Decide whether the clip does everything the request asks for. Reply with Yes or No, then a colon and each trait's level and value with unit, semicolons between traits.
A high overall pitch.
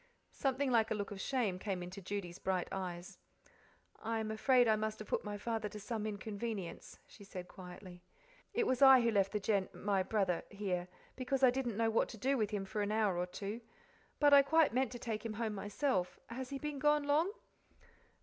Yes: high, 215 Hz